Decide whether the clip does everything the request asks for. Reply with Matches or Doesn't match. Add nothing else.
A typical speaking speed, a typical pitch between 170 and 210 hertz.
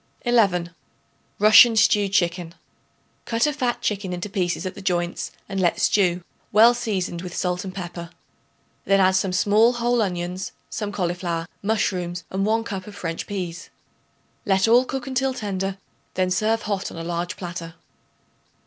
Matches